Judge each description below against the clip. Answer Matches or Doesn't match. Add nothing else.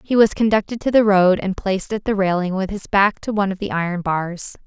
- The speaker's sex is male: Doesn't match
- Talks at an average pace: Doesn't match